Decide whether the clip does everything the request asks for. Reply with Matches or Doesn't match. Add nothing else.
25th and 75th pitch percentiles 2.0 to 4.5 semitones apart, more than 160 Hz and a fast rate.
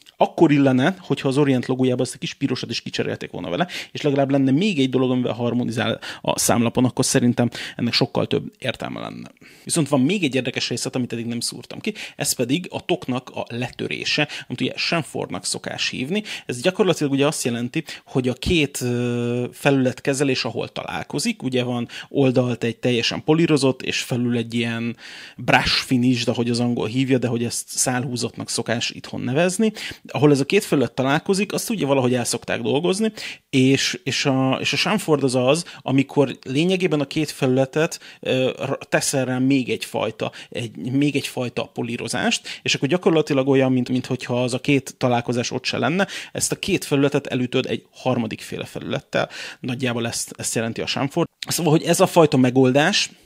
Doesn't match